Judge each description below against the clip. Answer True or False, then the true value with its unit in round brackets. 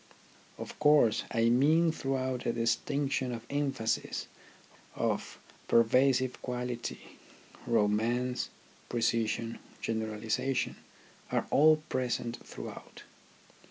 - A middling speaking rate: False (90 wpm)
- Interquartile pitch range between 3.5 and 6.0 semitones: False (2.8 semitones)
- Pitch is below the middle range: True (125 Hz)